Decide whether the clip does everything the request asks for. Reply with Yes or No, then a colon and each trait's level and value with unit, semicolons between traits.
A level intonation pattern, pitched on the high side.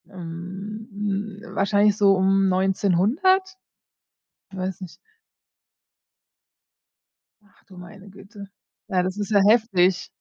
Yes: narrow, 2.0 semitones; high, 195 Hz